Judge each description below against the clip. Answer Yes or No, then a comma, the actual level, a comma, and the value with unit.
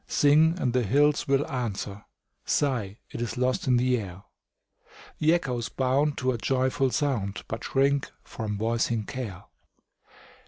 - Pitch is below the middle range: Yes, low, 125 Hz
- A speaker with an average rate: Yes, average, 145 wpm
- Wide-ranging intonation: No, average, 3.7 semitones